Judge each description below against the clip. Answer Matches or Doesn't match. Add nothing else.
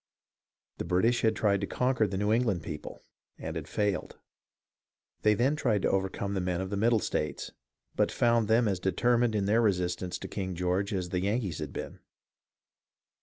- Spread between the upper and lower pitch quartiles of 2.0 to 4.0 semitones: Matches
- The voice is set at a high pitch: Doesn't match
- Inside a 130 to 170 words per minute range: Doesn't match